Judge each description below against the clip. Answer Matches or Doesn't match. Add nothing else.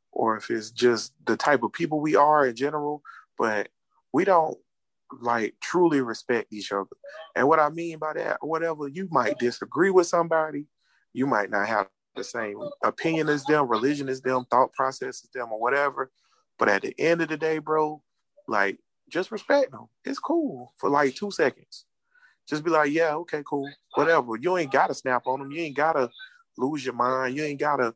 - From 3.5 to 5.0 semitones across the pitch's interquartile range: Matches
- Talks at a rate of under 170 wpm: Doesn't match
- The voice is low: Doesn't match